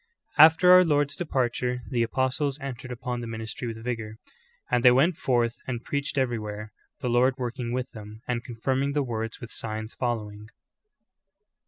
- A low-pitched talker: Yes, low, 125 Hz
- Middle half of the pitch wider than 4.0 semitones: No, average, 2.8 semitones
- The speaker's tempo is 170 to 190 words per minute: No, average, 160 wpm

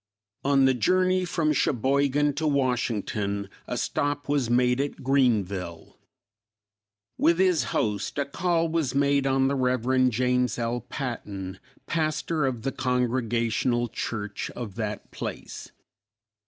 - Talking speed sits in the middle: No, slow, 125 wpm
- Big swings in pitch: No, average, 3.5 semitones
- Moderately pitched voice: No, low, 130 Hz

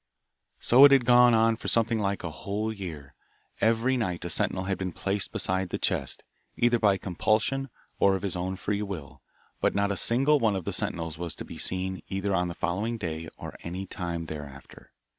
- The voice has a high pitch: No, very low, 95 Hz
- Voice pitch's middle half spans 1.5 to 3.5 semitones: No, average, 4.2 semitones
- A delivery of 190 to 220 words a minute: Yes, average, 200 wpm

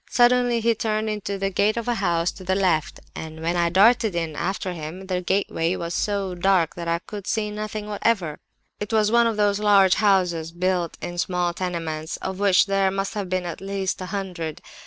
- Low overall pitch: No, high, 190 Hz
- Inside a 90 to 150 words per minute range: No, fast, 205 wpm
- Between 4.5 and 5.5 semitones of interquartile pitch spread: No, average, 3.1 semitones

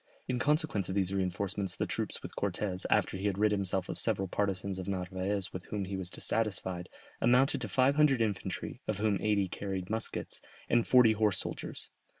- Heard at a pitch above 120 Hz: No, low, 100 Hz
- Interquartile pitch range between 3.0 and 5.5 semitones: No, narrow, 2.6 semitones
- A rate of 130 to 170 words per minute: No, average, 185 wpm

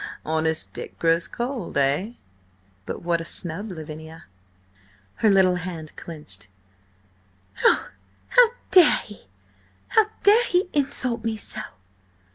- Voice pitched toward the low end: No, medium, 180 Hz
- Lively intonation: Yes, wide, 7.5 semitones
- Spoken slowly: Yes, slow, 115 wpm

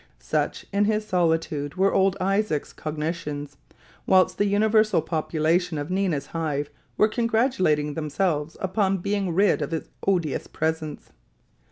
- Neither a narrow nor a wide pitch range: Yes, average, 4.4 semitones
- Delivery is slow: Yes, slow, 130 wpm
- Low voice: No, medium, 170 Hz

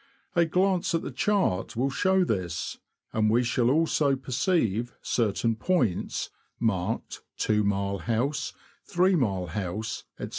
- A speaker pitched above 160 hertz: No, low, 120 Hz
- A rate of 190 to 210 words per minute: No, average, 140 wpm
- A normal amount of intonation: No, wide, 8.0 semitones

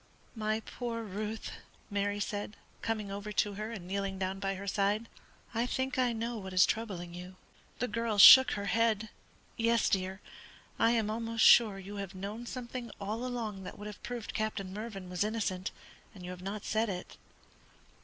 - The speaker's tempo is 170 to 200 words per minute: Yes, average, 180 wpm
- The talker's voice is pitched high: Yes, high, 210 Hz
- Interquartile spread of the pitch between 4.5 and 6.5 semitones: No, average, 2.8 semitones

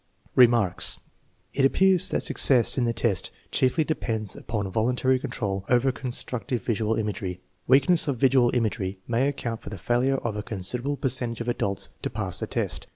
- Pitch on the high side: No, low, 120 Hz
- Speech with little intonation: No, average, 3.2 semitones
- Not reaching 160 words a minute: No, average, 165 wpm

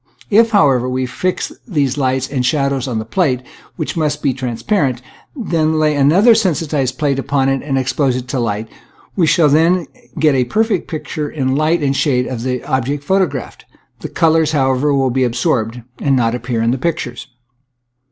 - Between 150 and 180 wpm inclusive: No, average, 190 wpm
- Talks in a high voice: No, medium, 140 Hz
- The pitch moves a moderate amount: Yes, average, 3.6 semitones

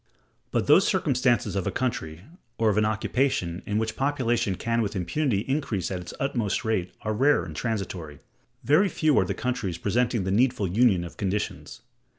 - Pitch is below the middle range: Yes, low, 110 Hz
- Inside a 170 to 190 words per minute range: Yes, average, 175 wpm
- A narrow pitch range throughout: No, average, 4.9 semitones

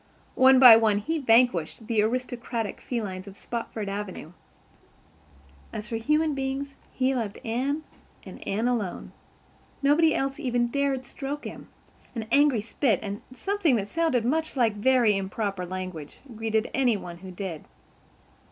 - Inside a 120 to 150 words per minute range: Yes, average, 145 wpm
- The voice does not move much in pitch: No, average, 4.7 semitones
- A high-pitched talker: Yes, high, 235 Hz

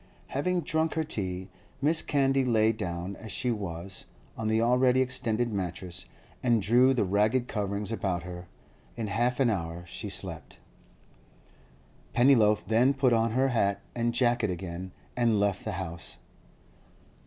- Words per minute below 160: Yes, average, 145 wpm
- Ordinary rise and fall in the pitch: Yes, average, 4.6 semitones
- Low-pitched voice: Yes, low, 110 Hz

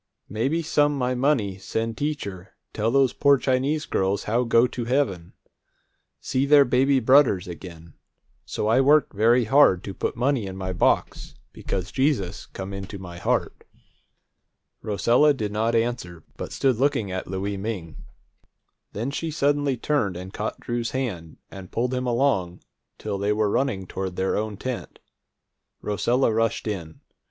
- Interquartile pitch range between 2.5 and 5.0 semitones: No, wide, 5.6 semitones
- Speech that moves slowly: No, average, 155 wpm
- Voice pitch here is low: Yes, low, 115 Hz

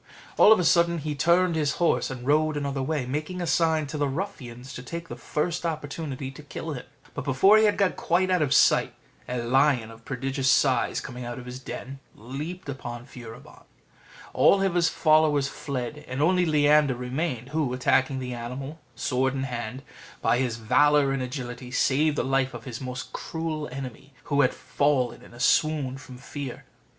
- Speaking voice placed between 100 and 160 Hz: Yes, medium, 140 Hz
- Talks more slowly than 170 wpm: No, average, 185 wpm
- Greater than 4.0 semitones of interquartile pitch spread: No, average, 3.5 semitones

